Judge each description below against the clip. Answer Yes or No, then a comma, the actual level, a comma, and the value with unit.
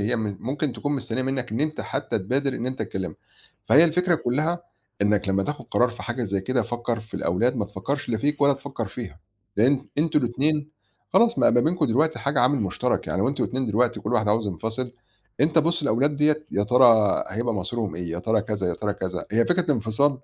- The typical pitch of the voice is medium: No, low, 125 Hz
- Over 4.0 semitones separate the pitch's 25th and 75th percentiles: Yes, average, 5.3 semitones